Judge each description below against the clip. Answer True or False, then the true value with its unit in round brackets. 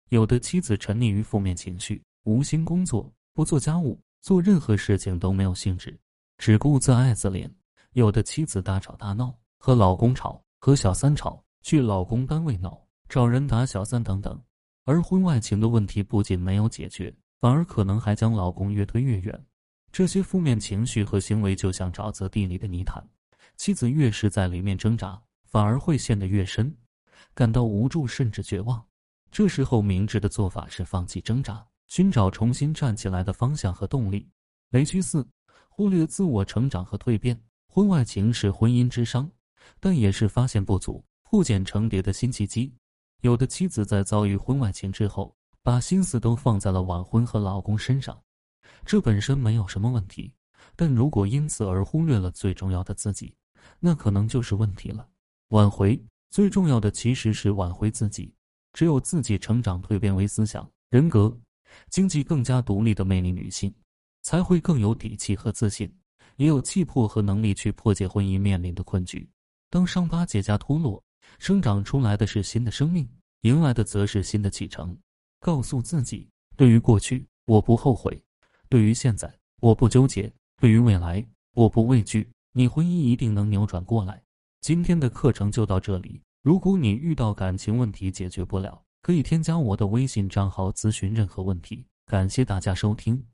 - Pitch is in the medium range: False (110 Hz)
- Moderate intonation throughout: True (4.4 semitones)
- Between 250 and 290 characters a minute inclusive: True (270 characters per minute)